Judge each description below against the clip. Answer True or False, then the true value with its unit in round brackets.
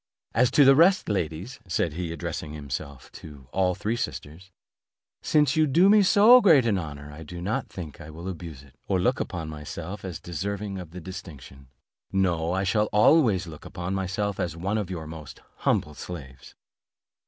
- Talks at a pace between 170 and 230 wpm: True (185 wpm)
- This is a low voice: True (90 Hz)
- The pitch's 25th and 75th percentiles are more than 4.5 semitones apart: True (5.1 semitones)